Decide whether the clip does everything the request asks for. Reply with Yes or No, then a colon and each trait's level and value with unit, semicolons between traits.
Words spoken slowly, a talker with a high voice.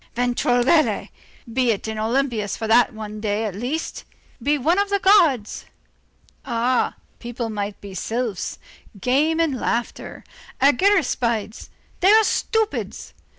Yes: slow, 120 wpm; high, 245 Hz